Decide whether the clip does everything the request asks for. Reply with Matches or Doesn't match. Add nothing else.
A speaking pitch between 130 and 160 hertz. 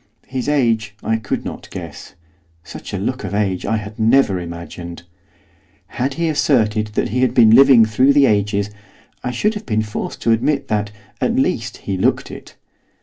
Doesn't match